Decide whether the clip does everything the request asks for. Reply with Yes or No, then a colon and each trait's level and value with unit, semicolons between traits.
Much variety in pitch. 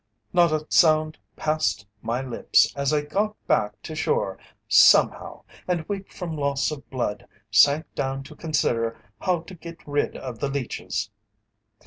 No: average, 3.6 semitones